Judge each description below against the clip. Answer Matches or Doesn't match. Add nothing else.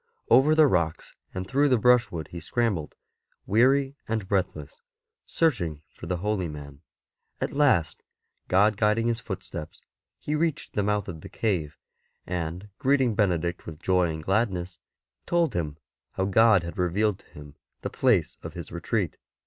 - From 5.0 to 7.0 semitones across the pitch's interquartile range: Matches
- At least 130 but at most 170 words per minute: Matches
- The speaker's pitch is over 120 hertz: Doesn't match